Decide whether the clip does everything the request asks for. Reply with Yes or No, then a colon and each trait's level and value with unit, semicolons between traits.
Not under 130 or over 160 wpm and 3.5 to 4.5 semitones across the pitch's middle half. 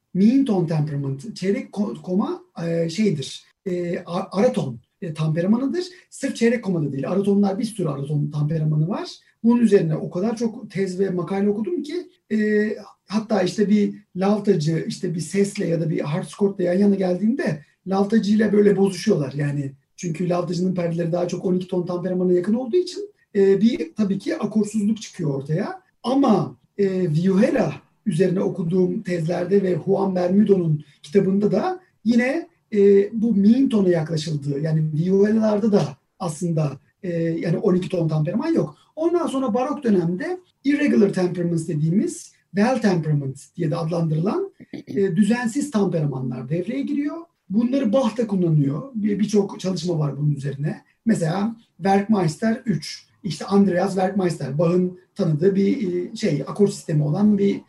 Yes: average, 135 wpm; average, 4.0 semitones